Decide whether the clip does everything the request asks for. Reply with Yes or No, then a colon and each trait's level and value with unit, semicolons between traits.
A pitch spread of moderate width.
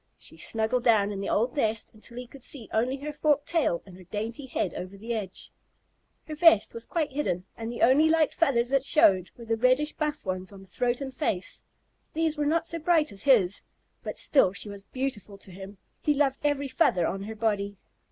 No: wide, 6.4 semitones